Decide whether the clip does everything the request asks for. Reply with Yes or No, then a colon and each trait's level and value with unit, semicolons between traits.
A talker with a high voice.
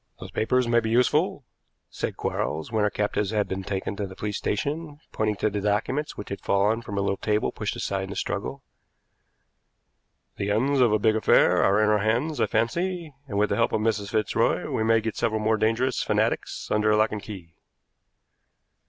No: low, 110 Hz